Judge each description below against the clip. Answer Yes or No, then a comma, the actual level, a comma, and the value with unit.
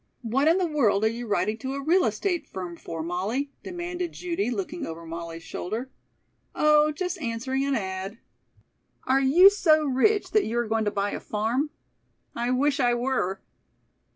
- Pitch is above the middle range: Yes, very high, 260 Hz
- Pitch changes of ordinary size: No, wide, 6.5 semitones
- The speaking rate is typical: Yes, average, 175 wpm